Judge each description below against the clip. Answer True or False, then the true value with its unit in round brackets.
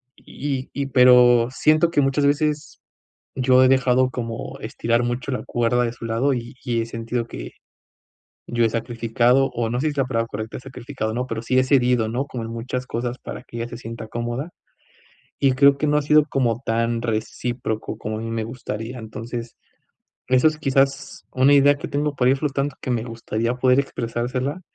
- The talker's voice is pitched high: False (125 Hz)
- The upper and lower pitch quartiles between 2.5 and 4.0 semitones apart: True (2.8 semitones)